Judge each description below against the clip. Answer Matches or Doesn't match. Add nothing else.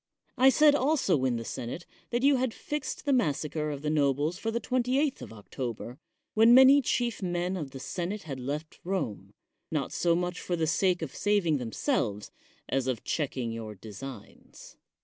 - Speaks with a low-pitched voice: Doesn't match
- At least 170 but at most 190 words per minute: Matches